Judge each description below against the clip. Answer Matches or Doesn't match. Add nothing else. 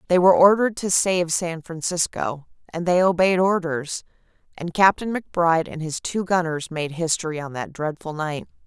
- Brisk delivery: Doesn't match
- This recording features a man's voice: Doesn't match